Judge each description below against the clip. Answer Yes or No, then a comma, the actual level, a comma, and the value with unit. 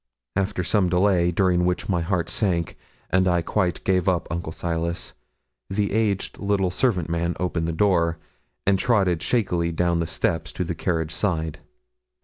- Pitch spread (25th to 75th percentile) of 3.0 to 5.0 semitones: No, narrow, 2.4 semitones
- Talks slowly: No, average, 160 wpm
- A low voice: Yes, very low, 90 Hz